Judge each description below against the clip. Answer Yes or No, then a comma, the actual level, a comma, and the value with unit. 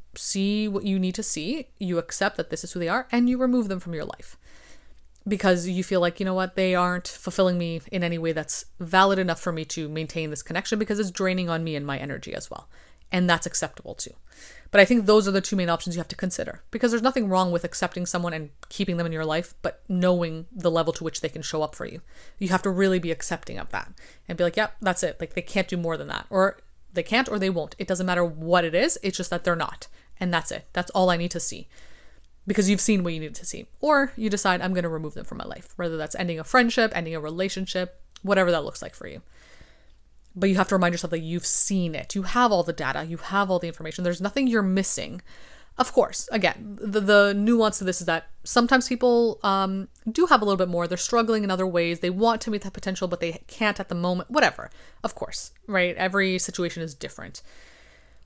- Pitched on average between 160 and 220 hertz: Yes, medium, 185 Hz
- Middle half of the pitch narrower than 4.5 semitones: Yes, average, 3.0 semitones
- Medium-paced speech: No, fast, 250 wpm